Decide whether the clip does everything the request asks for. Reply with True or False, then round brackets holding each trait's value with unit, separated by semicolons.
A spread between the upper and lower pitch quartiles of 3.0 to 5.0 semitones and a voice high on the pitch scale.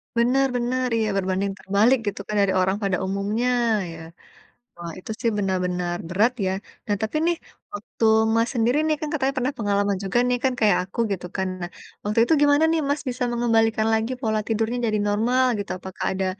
True (4.1 semitones; 220 Hz)